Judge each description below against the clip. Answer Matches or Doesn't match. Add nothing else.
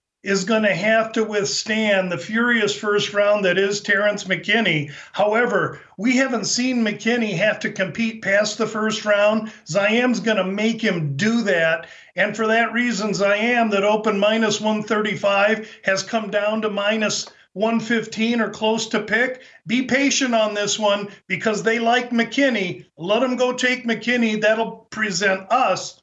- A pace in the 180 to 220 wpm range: Doesn't match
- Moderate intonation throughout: Doesn't match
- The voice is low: Doesn't match